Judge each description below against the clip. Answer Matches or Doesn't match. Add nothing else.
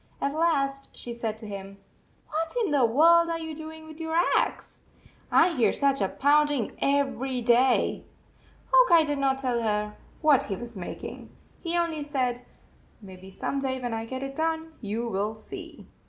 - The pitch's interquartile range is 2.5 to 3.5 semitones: Doesn't match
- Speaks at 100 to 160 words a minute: Doesn't match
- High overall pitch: Matches